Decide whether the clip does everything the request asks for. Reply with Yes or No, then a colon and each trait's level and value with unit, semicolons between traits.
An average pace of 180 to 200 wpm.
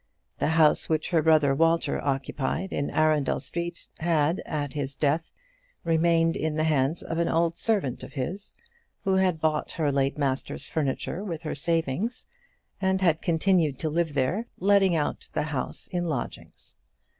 No: average, 160 wpm